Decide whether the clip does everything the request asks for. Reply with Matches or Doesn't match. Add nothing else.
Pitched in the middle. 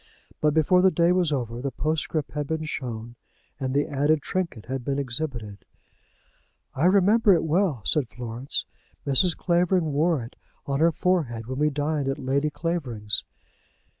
Matches